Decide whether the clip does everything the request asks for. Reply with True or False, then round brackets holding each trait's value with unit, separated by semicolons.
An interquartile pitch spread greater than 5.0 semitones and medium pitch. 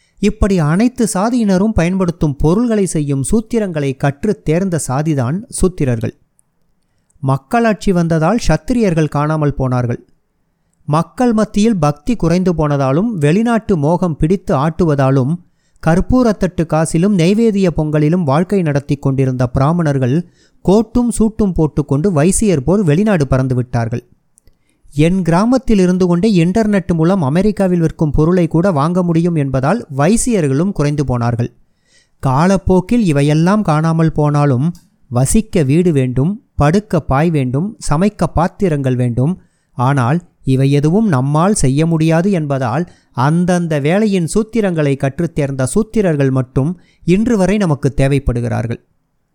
True (5.4 semitones; 165 Hz)